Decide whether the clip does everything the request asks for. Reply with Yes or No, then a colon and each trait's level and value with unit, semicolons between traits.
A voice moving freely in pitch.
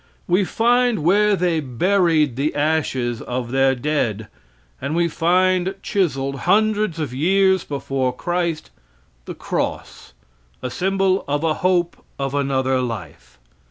Yes: wide, 5.8 semitones